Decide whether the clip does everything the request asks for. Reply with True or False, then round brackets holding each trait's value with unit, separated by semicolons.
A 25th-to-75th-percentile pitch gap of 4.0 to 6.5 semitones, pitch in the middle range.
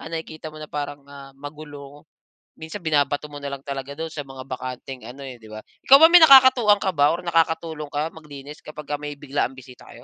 False (2.5 semitones; 145 Hz)